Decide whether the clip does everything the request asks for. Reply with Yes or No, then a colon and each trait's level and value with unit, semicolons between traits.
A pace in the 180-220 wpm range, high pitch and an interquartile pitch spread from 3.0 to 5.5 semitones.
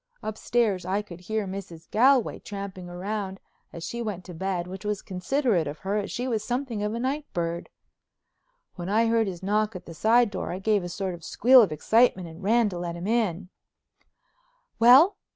Yes: average, 195 wpm; high, 200 Hz; average, 4.1 semitones